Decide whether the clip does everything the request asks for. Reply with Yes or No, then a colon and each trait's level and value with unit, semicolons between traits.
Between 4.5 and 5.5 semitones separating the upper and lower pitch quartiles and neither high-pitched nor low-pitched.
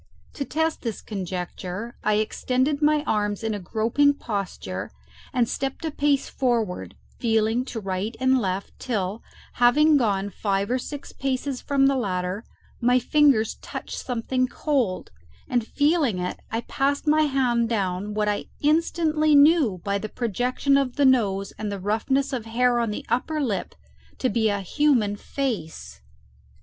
No: average, 5.2 semitones; high, 240 Hz